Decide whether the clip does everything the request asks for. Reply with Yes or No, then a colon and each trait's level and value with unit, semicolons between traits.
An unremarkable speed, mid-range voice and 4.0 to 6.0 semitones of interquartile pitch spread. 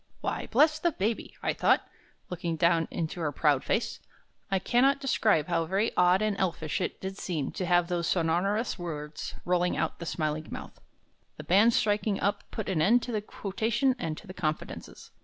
Yes: average, 195 wpm; medium, 180 Hz; average, 4.6 semitones